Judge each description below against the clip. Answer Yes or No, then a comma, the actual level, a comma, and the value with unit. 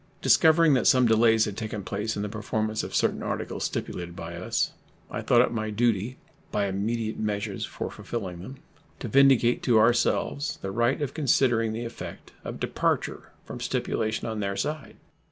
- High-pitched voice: No, low, 110 Hz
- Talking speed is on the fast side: No, average, 170 wpm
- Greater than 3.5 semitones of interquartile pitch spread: No, average, 2.7 semitones